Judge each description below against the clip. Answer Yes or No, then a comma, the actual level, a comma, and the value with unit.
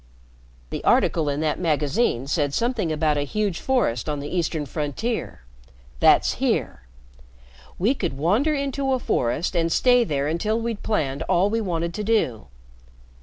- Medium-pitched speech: Yes, medium, 170 Hz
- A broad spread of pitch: Yes, wide, 7.5 semitones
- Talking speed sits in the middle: Yes, average, 155 wpm